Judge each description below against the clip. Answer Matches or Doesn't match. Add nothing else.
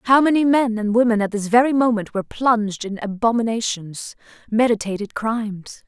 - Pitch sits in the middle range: Doesn't match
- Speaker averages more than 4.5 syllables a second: Matches